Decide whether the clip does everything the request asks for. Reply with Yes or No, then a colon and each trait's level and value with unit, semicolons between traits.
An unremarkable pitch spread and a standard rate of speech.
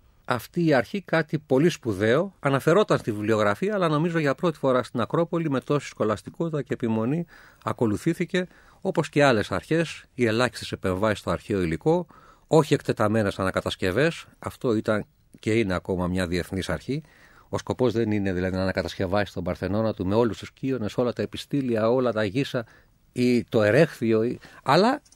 No: wide, 6.2 semitones; average, 160 wpm